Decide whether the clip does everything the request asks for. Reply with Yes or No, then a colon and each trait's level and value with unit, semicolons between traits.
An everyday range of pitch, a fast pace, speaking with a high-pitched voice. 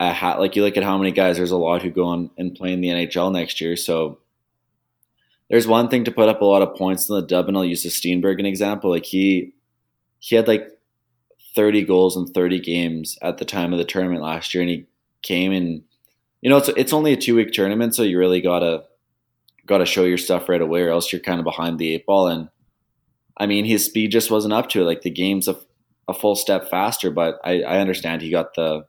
No: average, 3.1 semitones; fast, 250 wpm; very low, 90 Hz